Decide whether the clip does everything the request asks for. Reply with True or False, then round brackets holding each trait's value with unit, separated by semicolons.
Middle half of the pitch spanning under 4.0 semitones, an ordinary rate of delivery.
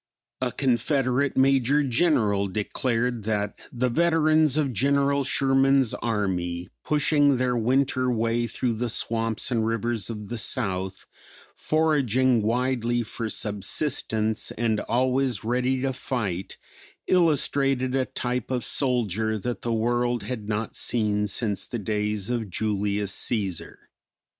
False (3.6 semitones; 125 wpm)